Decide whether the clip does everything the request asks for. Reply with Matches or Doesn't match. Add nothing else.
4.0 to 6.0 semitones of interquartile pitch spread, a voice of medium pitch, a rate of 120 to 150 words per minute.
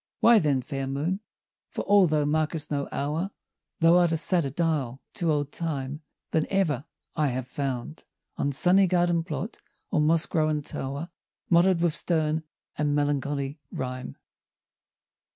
Doesn't match